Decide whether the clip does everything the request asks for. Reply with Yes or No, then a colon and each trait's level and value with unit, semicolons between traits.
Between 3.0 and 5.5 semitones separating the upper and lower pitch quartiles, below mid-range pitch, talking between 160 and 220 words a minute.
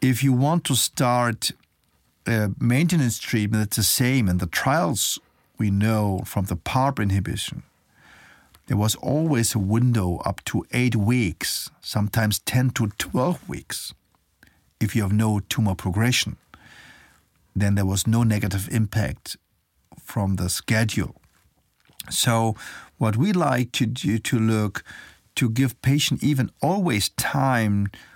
No: average, 3.6 semitones; low, 110 Hz; average, 135 wpm